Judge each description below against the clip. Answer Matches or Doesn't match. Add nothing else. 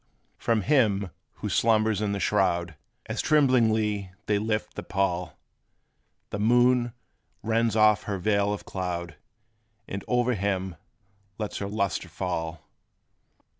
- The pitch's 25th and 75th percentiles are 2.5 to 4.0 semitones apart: Matches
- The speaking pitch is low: Matches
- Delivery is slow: Matches